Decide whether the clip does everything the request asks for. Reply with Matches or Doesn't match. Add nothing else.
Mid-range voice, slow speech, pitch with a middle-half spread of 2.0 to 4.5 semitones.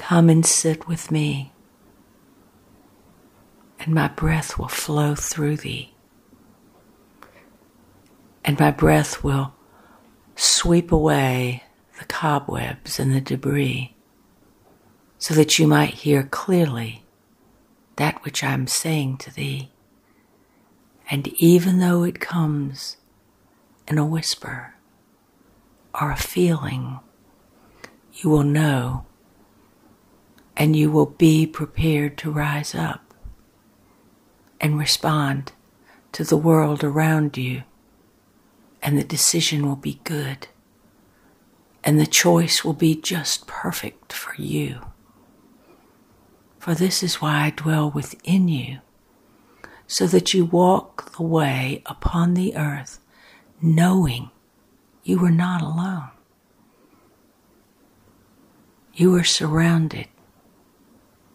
Matches